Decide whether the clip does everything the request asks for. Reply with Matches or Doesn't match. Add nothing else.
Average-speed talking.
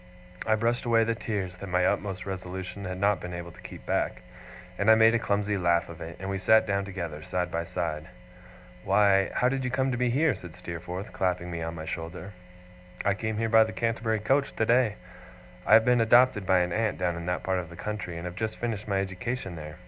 Doesn't match